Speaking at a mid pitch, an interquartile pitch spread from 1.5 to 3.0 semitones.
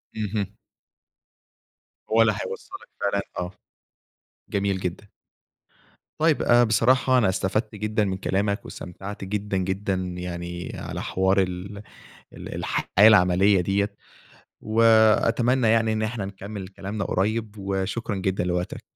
No: low, 100 Hz; narrow, 2.5 semitones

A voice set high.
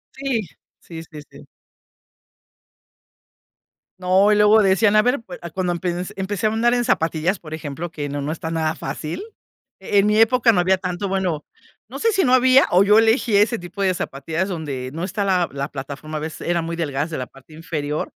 No: medium, 180 Hz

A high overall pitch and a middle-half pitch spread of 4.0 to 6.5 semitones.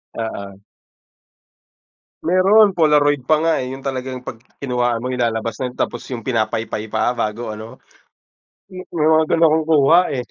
No: low, 130 Hz; wide, 5.4 semitones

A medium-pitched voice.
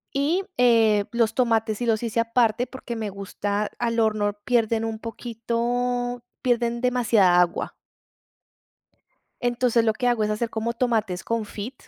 No: high, 230 Hz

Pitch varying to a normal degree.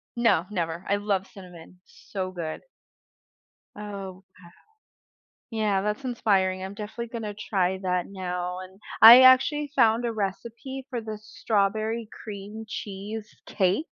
Yes: average, 3.0 semitones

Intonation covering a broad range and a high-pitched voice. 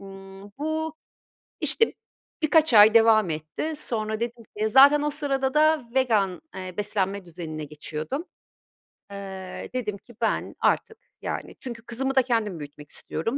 Yes: wide, 5.7 semitones; high, 220 Hz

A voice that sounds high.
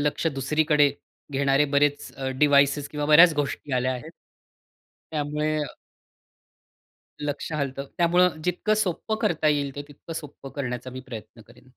No: medium, 145 Hz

